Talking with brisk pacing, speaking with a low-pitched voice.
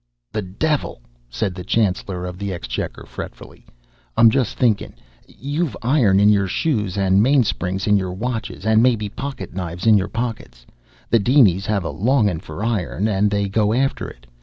No: average, 170 wpm; low, 105 Hz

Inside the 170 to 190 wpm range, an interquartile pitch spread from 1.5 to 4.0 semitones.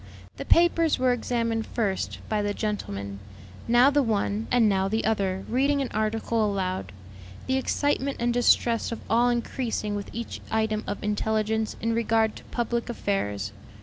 No: average, 155 wpm; average, 2.7 semitones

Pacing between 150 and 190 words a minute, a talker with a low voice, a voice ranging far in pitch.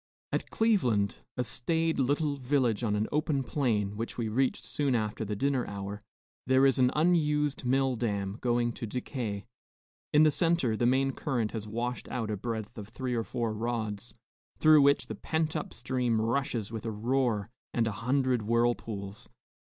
No: average, 175 wpm; low, 120 Hz; average, 3.8 semitones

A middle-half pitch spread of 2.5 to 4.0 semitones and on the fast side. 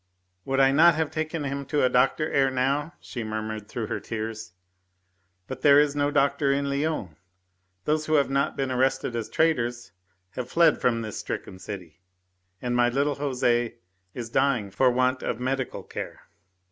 No: average, 3.2 semitones; average, 170 wpm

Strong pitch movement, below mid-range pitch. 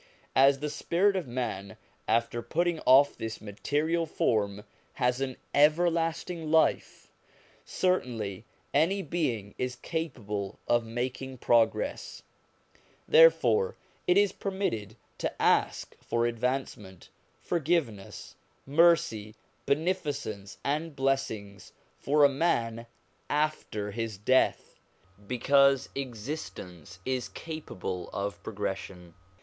Yes: wide, 6.6 semitones; low, 130 Hz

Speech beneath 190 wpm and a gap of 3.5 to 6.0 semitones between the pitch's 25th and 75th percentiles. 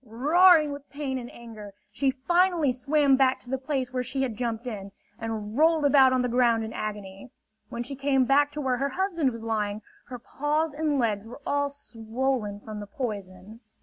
No: average, 195 wpm; average, 4.2 semitones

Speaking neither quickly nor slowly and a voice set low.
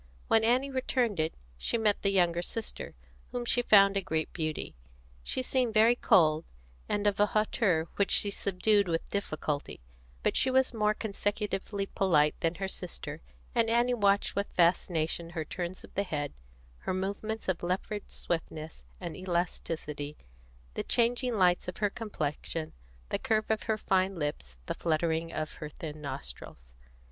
No: average, 160 wpm; high, 190 Hz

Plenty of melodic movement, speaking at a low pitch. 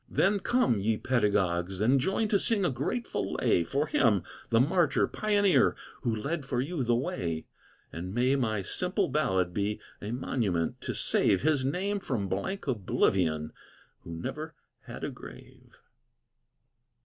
Yes: wide, 8.5 semitones; low, 125 Hz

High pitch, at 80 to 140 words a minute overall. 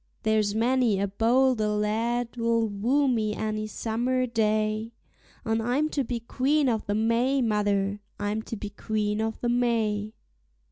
Yes: high, 225 Hz; slow, 135 wpm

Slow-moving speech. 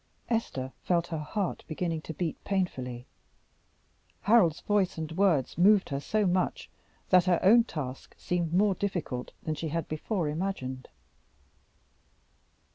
Yes: slow, 130 wpm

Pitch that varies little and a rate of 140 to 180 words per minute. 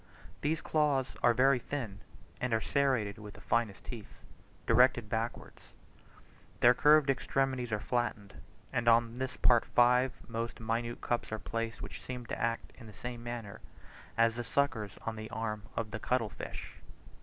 Yes: narrow, 2.2 semitones; average, 165 wpm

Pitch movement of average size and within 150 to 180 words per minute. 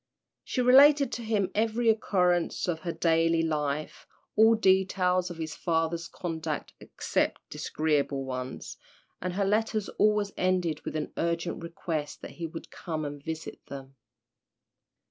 No: average, 4.2 semitones; average, 140 wpm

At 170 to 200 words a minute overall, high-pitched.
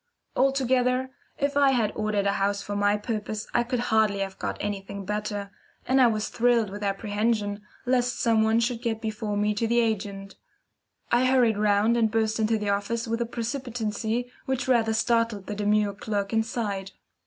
Yes: average, 175 wpm; high, 220 Hz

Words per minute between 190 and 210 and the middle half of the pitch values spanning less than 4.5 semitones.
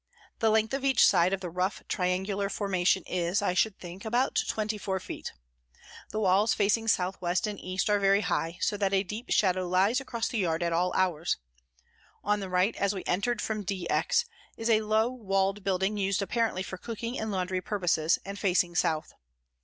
Yes: average, 200 wpm; average, 2.8 semitones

